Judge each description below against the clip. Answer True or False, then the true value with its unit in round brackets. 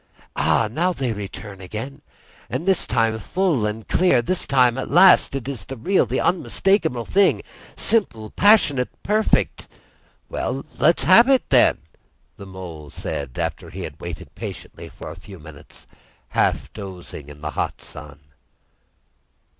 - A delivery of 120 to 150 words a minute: True (140 wpm)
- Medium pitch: False (120 Hz)